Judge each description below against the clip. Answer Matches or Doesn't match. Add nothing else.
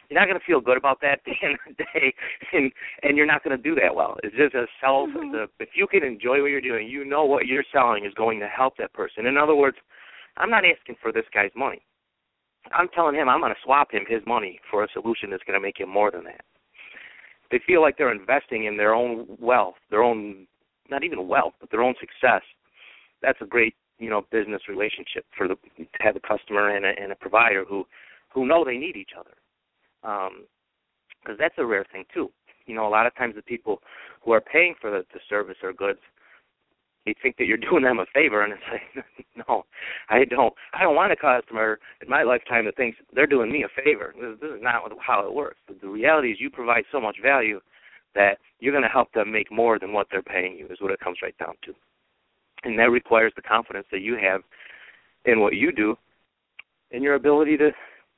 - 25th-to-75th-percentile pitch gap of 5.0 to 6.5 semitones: Matches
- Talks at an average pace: Doesn't match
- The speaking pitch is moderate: Doesn't match